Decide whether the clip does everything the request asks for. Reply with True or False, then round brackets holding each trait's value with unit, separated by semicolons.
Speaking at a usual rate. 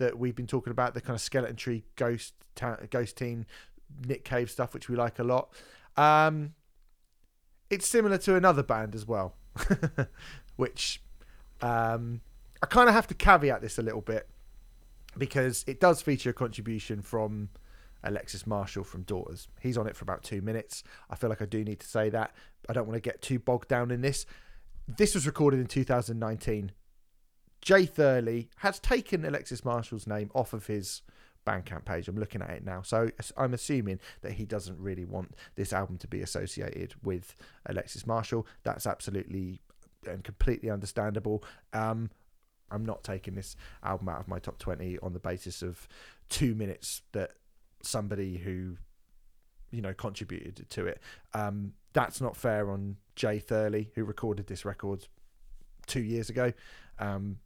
True (170 wpm)